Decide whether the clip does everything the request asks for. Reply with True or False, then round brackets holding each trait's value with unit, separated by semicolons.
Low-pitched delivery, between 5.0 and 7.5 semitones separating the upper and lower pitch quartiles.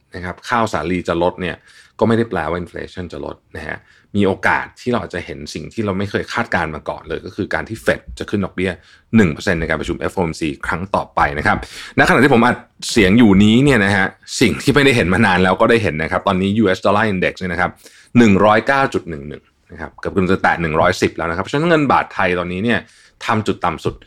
False (95 Hz; 3.7 semitones)